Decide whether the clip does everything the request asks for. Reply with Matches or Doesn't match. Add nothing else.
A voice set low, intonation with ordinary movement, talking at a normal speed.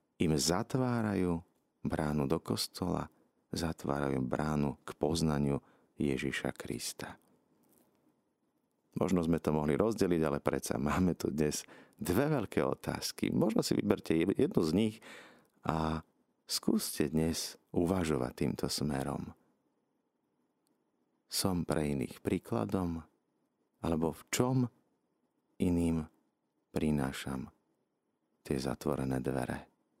Doesn't match